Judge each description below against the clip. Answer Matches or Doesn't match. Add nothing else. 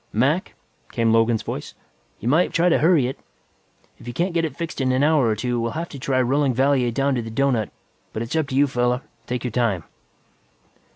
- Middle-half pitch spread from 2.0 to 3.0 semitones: Doesn't match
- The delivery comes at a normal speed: Doesn't match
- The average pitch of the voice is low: Matches